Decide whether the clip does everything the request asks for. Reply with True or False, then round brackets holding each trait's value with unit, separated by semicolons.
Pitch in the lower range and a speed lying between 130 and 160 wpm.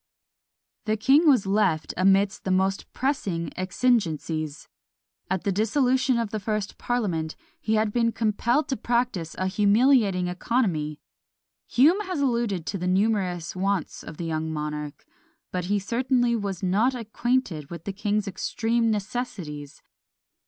False (205 Hz; 140 wpm)